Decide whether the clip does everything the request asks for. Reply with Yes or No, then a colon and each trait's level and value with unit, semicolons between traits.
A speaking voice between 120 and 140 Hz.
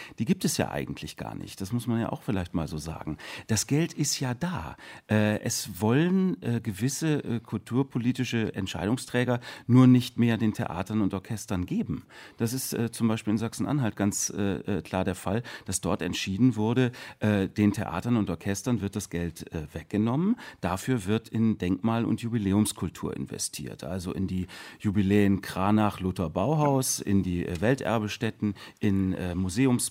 No: low, 110 Hz